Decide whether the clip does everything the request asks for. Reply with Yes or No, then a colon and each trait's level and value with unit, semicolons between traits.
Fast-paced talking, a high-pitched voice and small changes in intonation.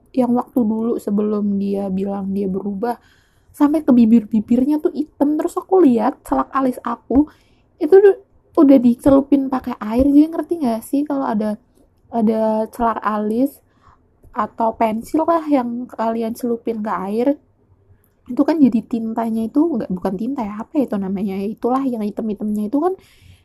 No: fast, 155 wpm; high, 235 Hz; average, 4.7 semitones